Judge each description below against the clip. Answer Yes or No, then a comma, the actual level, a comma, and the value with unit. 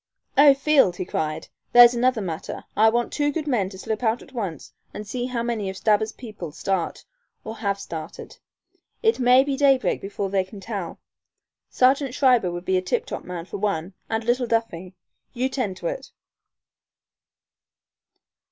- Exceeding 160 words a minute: Yes, average, 170 wpm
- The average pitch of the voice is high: Yes, high, 220 Hz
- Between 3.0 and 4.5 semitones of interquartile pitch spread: No, average, 5.0 semitones